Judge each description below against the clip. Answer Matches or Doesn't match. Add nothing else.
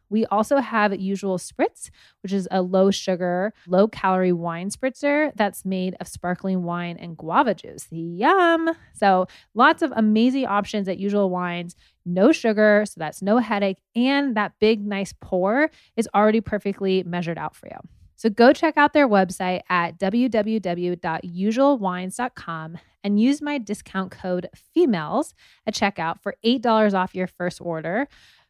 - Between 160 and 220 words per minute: Doesn't match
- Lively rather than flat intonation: Doesn't match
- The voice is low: Doesn't match